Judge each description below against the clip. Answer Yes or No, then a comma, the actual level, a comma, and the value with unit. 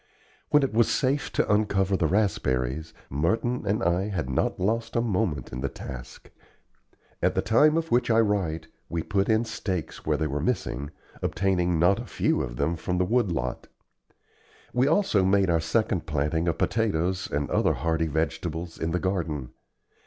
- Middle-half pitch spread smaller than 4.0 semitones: No, wide, 5.5 semitones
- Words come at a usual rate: Yes, average, 175 wpm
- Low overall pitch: Yes, very low, 90 Hz